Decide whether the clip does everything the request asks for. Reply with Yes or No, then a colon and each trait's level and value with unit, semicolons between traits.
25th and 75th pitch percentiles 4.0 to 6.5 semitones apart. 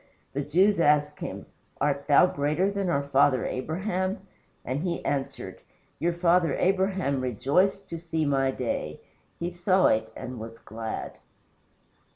Yes: average, 5.2 semitones